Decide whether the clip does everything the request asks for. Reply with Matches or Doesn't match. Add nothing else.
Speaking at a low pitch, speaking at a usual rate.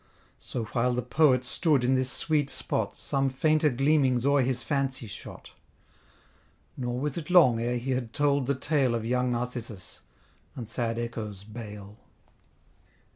Matches